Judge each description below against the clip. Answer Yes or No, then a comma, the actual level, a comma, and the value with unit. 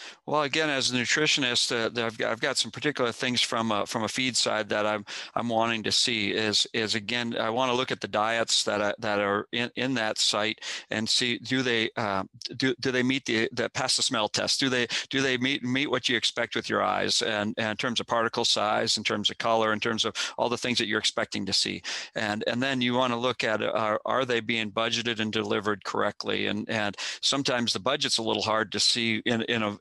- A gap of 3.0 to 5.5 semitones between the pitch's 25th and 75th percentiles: No, narrow, 2.6 semitones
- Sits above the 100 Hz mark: Yes, low, 115 Hz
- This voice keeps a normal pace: No, fast, 245 wpm